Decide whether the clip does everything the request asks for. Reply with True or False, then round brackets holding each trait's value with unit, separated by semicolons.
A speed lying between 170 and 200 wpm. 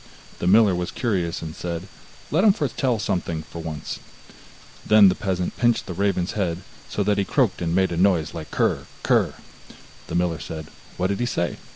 True (190 wpm)